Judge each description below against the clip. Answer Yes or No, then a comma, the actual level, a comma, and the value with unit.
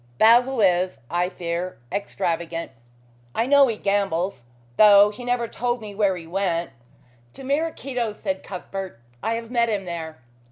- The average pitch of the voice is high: Yes, high, 200 Hz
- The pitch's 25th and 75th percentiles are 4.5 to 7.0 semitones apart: Yes, average, 5.0 semitones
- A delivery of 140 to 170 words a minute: Yes, average, 155 wpm